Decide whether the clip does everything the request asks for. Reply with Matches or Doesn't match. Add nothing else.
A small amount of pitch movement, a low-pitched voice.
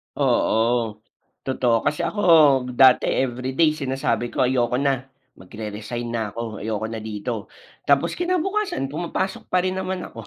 Doesn't match